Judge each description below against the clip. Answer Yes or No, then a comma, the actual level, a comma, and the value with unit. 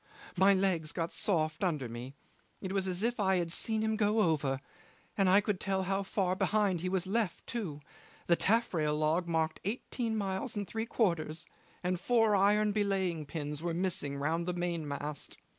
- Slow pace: No, average, 175 wpm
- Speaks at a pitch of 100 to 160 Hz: No, medium, 185 Hz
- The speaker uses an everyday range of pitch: Yes, average, 4.2 semitones